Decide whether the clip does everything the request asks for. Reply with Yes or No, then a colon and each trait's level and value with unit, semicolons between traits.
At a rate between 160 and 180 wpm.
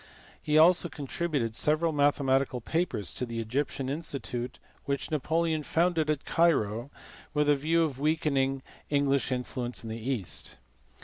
No: average, 140 wpm